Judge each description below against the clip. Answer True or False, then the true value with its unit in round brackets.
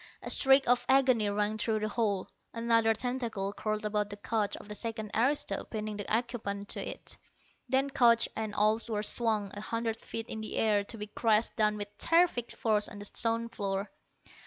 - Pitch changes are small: True (1.9 semitones)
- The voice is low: False (220 Hz)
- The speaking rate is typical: True (190 wpm)